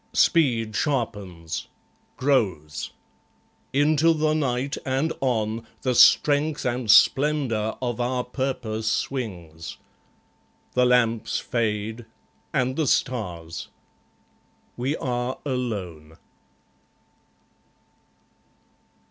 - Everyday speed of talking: No, slow, 80 wpm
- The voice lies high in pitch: No, low, 125 Hz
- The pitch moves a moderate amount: Yes, average, 4.0 semitones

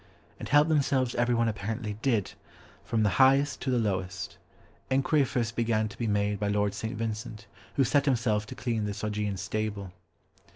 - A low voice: Yes, low, 110 Hz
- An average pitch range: Yes, average, 3.3 semitones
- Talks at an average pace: Yes, average, 170 wpm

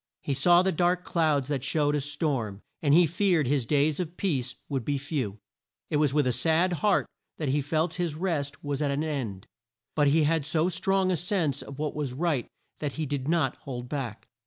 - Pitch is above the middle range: No, medium, 150 Hz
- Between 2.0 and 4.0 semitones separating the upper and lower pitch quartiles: Yes, average, 3.3 semitones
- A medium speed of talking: No, fast, 210 wpm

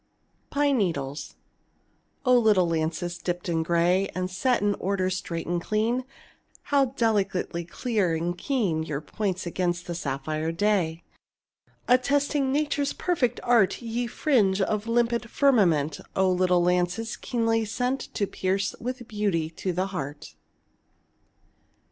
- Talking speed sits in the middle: No, slow, 130 wpm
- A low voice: No, high, 190 Hz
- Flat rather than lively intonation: No, wide, 5.5 semitones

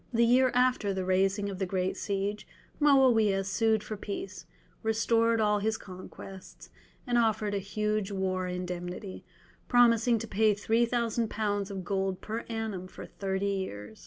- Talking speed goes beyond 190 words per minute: No, average, 150 wpm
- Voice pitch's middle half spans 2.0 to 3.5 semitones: Yes, average, 2.8 semitones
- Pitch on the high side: Yes, high, 205 Hz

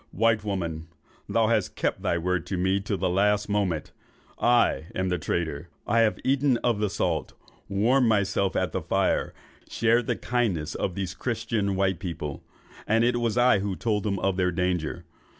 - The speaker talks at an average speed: Yes, average, 180 wpm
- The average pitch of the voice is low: Yes, low, 100 Hz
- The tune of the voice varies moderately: Yes, average, 3.9 semitones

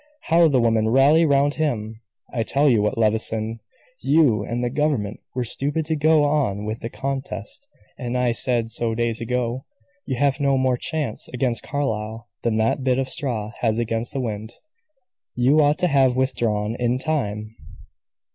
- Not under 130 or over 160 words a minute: No, average, 170 wpm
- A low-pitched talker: Yes, low, 125 Hz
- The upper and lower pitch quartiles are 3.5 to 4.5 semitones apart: Yes, average, 3.8 semitones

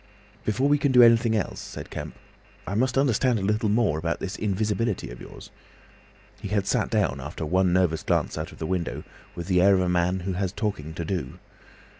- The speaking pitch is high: No, very low, 95 Hz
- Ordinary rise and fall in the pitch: Yes, average, 4.0 semitones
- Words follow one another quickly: Yes, fast, 210 wpm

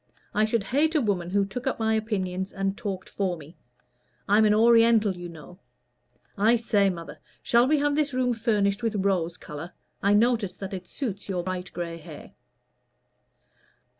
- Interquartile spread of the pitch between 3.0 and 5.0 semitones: Yes, average, 3.8 semitones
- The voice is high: Yes, high, 200 Hz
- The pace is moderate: Yes, average, 170 wpm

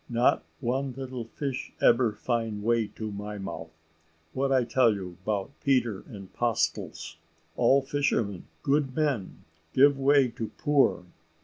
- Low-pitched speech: Yes, low, 120 Hz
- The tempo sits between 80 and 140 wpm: Yes, slow, 135 wpm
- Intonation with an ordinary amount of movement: Yes, average, 4.4 semitones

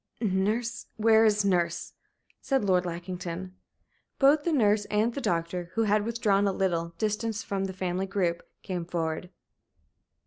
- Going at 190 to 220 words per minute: No, average, 145 wpm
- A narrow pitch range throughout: No, average, 3.7 semitones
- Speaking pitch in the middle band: No, high, 195 Hz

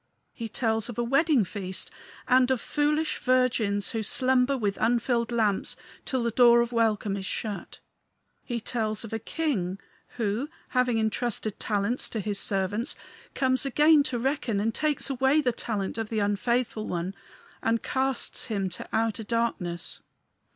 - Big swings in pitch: No, average, 3.4 semitones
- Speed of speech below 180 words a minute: Yes, average, 155 wpm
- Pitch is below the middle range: No, high, 230 Hz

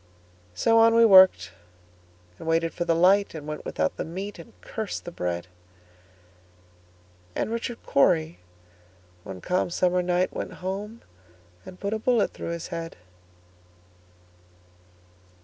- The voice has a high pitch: No, medium, 170 Hz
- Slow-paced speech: Yes, slow, 120 wpm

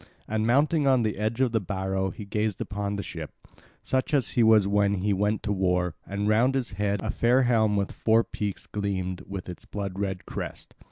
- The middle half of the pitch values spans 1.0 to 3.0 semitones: Yes, narrow, 2.5 semitones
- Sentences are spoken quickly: Yes, fast, 210 wpm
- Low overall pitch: Yes, low, 105 Hz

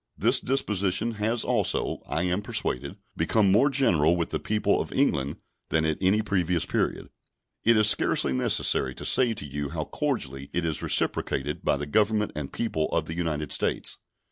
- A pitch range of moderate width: No, wide, 6.5 semitones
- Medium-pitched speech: No, very low, 90 Hz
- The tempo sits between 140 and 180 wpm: Yes, average, 175 wpm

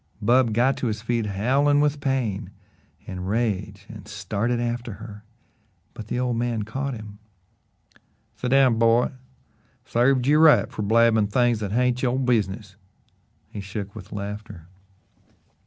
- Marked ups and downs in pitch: No, average, 3.2 semitones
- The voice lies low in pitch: Yes, low, 115 Hz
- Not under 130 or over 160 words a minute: Yes, average, 140 wpm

